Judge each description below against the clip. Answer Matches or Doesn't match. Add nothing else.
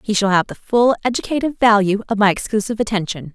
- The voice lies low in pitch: Doesn't match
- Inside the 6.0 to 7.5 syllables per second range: Matches